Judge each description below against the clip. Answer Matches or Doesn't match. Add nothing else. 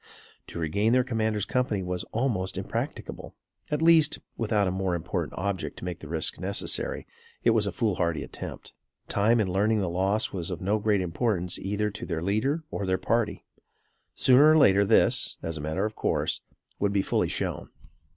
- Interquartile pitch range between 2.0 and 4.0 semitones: Matches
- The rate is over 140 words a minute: Matches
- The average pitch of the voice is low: Matches